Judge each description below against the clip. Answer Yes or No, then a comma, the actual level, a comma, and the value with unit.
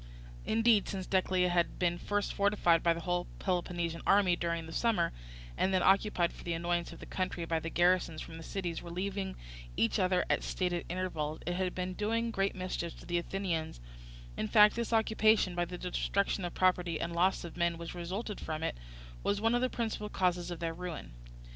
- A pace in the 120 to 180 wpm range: No, average, 200 wpm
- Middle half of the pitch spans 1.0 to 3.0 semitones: Yes, narrow, 2.5 semitones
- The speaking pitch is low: No, medium, 180 Hz